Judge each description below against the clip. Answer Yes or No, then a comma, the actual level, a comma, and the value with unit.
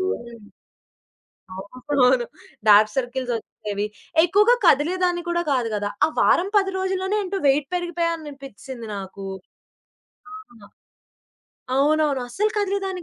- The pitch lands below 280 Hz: No, very high, 295 Hz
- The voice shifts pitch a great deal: Yes, wide, 7.5 semitones